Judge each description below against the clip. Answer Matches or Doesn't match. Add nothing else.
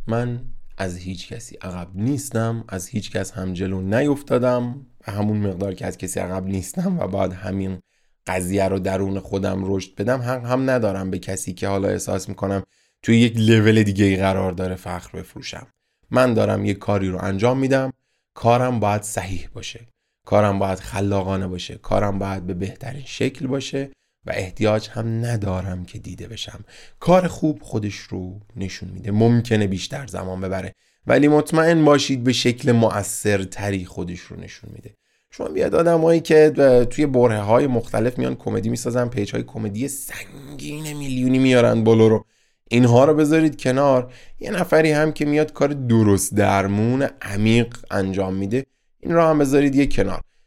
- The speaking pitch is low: Matches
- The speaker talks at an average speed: Doesn't match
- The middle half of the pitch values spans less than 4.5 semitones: Doesn't match